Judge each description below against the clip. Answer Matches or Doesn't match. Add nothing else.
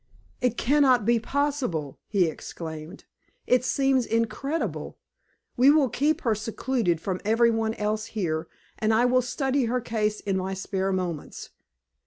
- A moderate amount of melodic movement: Matches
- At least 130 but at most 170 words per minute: Matches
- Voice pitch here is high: Matches